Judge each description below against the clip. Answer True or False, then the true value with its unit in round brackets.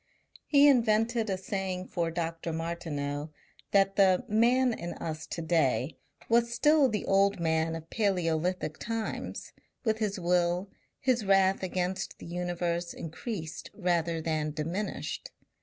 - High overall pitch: False (180 Hz)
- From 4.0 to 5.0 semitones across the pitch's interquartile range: True (4.4 semitones)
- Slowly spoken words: True (130 wpm)